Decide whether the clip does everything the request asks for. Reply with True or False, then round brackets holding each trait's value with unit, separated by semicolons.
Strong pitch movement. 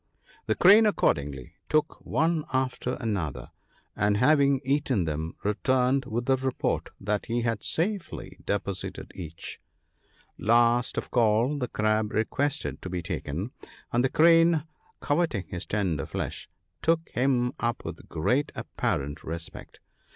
True (5.9 semitones)